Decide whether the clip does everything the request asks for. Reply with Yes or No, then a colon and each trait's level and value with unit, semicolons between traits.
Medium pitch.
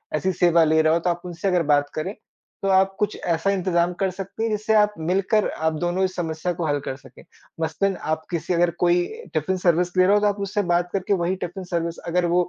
Yes: medium, 180 Hz